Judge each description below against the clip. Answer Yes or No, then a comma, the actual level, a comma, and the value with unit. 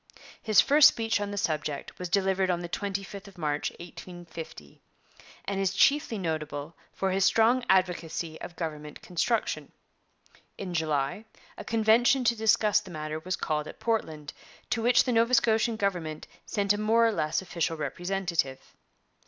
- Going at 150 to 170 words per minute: Yes, average, 155 wpm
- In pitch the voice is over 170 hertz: Yes, high, 190 Hz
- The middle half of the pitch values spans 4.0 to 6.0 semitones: Yes, wide, 5.4 semitones